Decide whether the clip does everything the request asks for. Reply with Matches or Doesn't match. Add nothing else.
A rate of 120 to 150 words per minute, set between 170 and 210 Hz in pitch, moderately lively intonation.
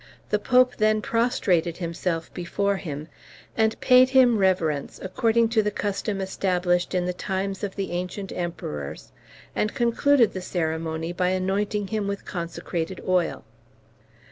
Matches